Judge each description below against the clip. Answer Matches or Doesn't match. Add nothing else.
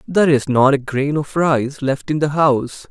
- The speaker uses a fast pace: Matches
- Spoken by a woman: Doesn't match